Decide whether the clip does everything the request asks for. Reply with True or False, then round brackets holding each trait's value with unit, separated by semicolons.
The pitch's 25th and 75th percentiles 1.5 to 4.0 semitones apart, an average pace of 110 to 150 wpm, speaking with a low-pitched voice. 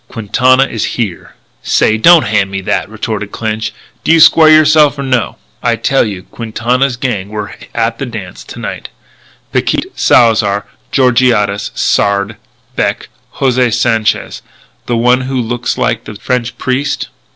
True (3.4 semitones; 145 wpm; 120 Hz)